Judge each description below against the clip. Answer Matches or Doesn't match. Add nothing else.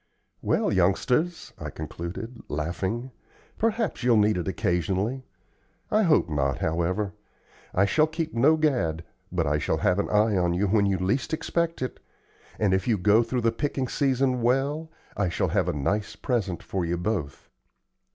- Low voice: Matches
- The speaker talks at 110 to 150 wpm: Doesn't match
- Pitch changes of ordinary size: Doesn't match